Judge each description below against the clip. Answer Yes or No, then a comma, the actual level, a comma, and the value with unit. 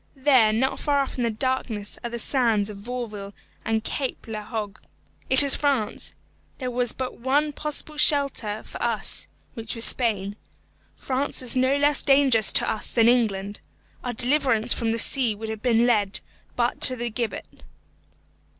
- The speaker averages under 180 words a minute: Yes, average, 165 wpm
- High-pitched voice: Yes, high, 240 Hz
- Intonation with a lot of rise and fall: No, average, 3.4 semitones